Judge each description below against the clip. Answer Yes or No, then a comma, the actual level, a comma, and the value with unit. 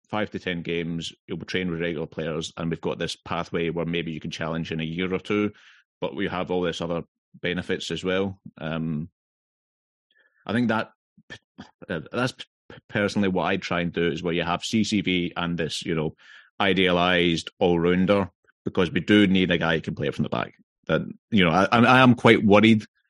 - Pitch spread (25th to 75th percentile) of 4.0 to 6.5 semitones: No, average, 2.7 semitones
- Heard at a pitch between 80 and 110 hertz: Yes, very low, 90 Hz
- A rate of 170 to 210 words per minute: Yes, average, 200 wpm